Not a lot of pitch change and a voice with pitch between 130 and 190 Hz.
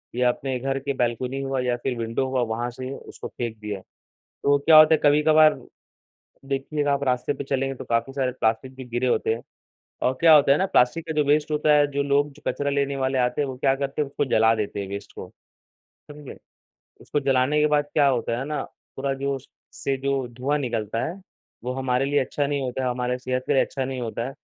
Yes: narrow, 2.3 semitones; low, 135 Hz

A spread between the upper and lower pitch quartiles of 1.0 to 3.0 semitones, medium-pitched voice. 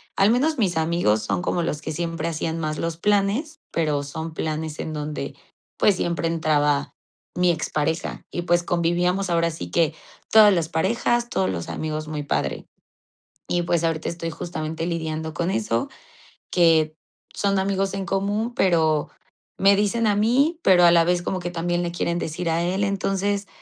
No: average, 3.6 semitones; medium, 170 Hz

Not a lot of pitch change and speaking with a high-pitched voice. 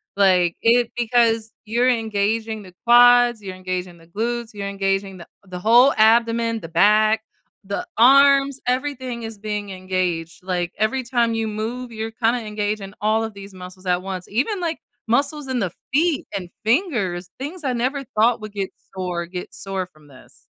No: average, 4.2 semitones; high, 220 Hz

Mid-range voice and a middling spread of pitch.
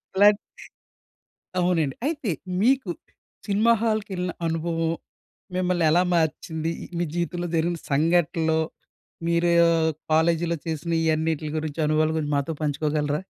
No: medium, 165 Hz; narrow, 2.3 semitones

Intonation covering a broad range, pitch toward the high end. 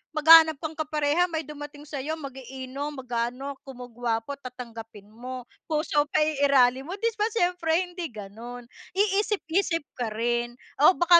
No: average, 4.6 semitones; very high, 285 Hz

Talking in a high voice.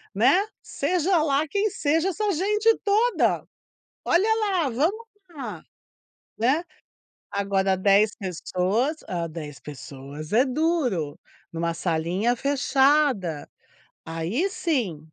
Yes: very high, 255 Hz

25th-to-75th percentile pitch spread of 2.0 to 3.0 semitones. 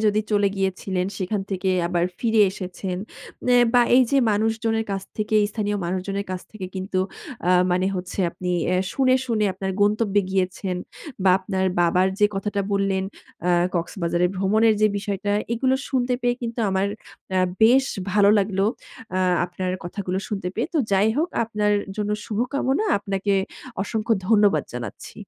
Yes: average, 2.7 semitones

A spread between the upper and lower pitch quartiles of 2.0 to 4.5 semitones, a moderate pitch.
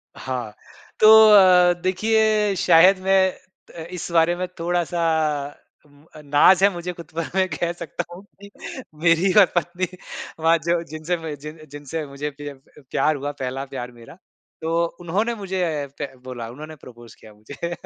Yes: average, 3.9 semitones; medium, 165 Hz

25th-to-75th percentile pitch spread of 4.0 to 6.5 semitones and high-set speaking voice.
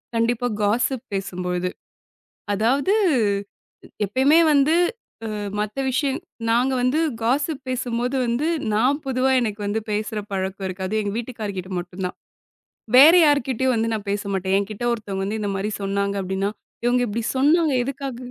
Yes: average, 4.7 semitones; high, 230 Hz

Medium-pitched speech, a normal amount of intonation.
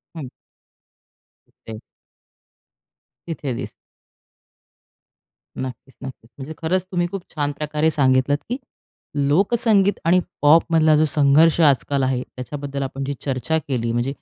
Yes: medium, 145 Hz; average, 3.5 semitones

